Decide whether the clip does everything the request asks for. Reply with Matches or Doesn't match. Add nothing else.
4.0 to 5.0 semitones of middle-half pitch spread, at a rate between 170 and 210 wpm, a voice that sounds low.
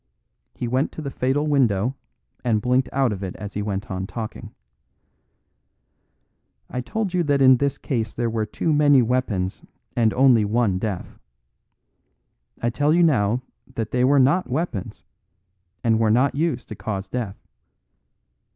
Doesn't match